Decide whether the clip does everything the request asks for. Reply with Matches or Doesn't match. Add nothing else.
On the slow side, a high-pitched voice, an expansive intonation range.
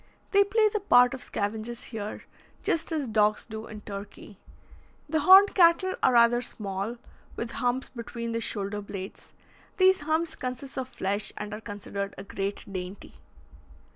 Doesn't match